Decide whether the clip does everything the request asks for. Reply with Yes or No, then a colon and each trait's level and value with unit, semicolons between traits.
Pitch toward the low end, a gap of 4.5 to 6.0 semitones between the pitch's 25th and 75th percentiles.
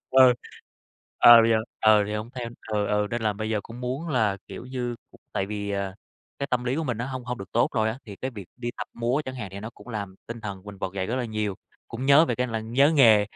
No: low, 115 Hz; average, 3.2 semitones